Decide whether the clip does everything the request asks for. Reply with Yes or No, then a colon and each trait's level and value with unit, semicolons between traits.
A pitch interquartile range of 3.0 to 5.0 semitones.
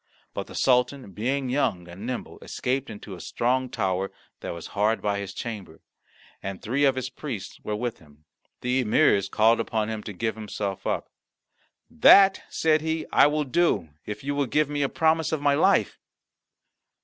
No: wide, 5.6 semitones